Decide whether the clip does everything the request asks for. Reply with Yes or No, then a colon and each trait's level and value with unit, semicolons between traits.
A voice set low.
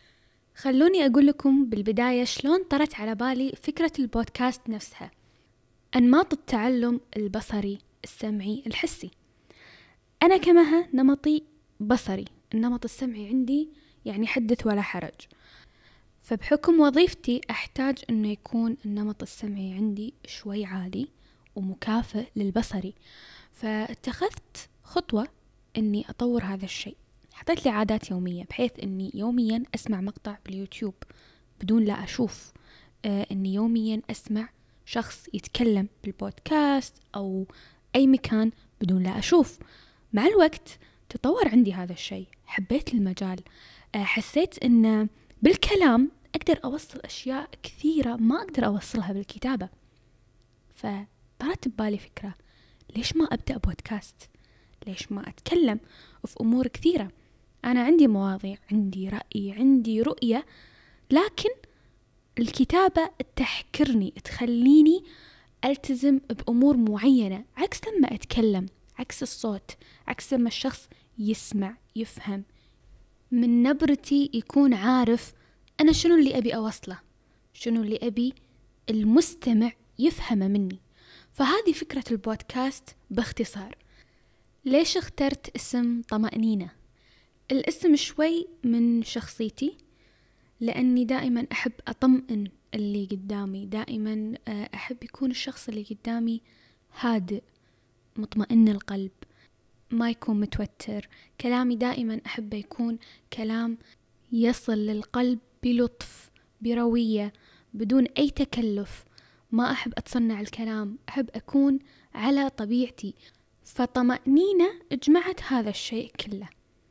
No: high, 230 Hz